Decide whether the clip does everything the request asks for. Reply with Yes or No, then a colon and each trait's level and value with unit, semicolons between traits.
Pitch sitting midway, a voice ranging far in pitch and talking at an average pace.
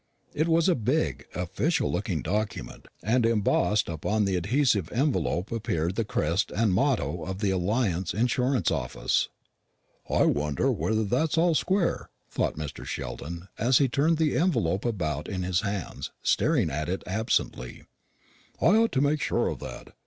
No: low, 105 Hz; wide, 7.2 semitones; average, 155 wpm